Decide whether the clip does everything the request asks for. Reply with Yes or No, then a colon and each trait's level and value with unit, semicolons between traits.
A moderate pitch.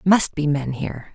Yes: medium, 155 Hz